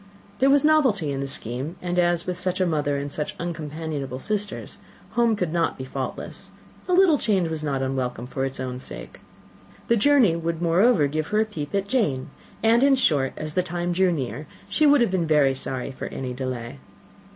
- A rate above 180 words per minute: Yes, average, 200 wpm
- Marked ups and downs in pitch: Yes, wide, 6.8 semitones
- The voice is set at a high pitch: No, medium, 165 Hz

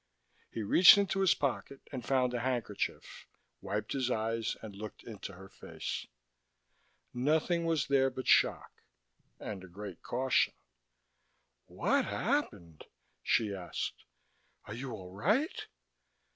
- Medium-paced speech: No, slow, 125 wpm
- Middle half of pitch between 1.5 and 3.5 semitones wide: No, average, 5.2 semitones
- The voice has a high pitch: No, low, 120 Hz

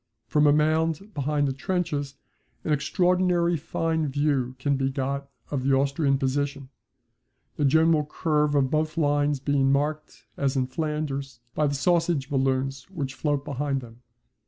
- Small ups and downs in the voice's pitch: Yes, narrow, 2.3 semitones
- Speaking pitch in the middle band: Yes, medium, 145 Hz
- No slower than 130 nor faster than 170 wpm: Yes, average, 150 wpm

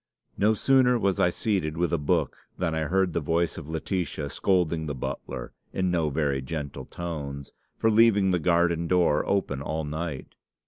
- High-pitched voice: No, very low, 85 Hz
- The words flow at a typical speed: Yes, average, 175 wpm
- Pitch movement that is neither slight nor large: Yes, average, 3.7 semitones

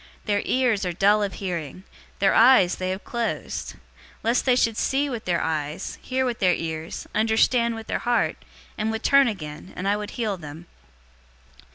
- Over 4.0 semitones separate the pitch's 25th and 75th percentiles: Yes, average, 4.7 semitones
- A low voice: No, high, 210 Hz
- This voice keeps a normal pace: Yes, average, 180 wpm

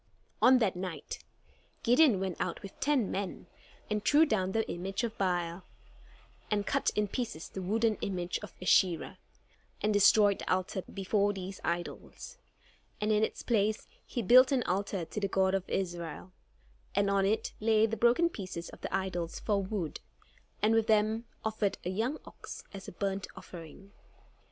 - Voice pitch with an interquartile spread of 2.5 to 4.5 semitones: Yes, average, 2.9 semitones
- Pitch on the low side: No, high, 200 Hz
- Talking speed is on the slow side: No, average, 165 wpm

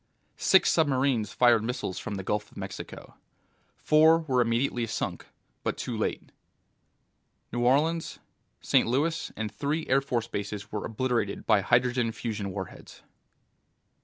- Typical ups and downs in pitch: Yes, average, 4.6 semitones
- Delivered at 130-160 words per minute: Yes, slow, 135 wpm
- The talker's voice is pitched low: Yes, low, 120 Hz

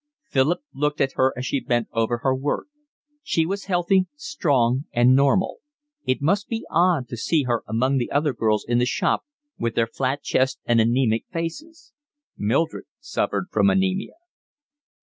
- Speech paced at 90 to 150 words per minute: No, average, 165 wpm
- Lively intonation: Yes, wide, 6.5 semitones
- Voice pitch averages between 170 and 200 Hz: No, low, 135 Hz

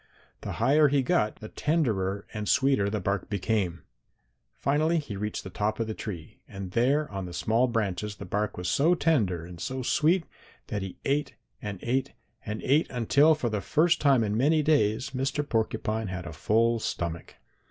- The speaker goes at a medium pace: Yes, average, 185 wpm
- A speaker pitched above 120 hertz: No, low, 110 Hz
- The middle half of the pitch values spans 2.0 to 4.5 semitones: No, wide, 5.6 semitones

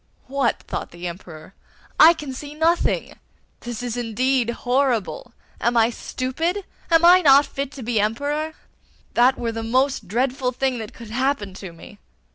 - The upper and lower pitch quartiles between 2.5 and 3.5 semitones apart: No, average, 3.9 semitones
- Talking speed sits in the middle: Yes, average, 160 wpm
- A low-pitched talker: No, very high, 255 Hz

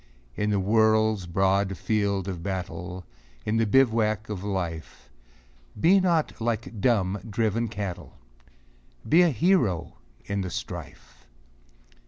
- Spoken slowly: Yes, slow, 120 wpm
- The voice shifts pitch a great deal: No, average, 3.1 semitones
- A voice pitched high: No, low, 105 Hz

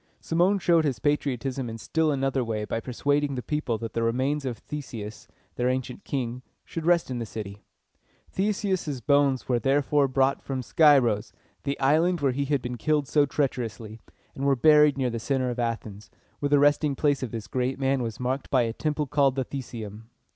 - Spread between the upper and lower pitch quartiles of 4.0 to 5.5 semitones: No, average, 3.5 semitones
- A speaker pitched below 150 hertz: Yes, low, 135 Hz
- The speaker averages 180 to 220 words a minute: Yes, average, 195 wpm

